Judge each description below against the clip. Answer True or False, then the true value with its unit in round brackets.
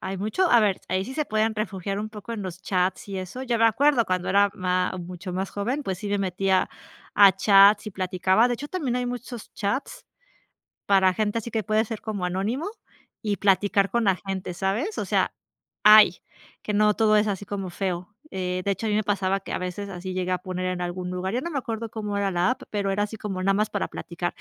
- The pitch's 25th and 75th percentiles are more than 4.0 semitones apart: False (2.7 semitones)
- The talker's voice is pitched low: False (200 Hz)